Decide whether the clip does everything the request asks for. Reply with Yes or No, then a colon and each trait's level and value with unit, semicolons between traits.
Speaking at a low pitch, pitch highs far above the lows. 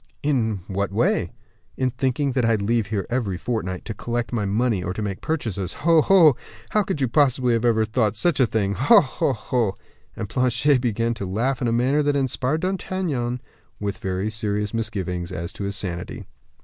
No: low, 115 Hz; average, 4.6 semitones